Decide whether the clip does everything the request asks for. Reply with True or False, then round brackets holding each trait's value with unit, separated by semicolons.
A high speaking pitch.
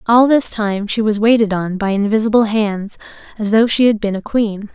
True (215 Hz)